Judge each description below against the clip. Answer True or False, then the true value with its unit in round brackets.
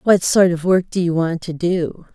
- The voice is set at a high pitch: False (175 Hz)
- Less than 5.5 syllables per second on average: True (4.5 syllables/s)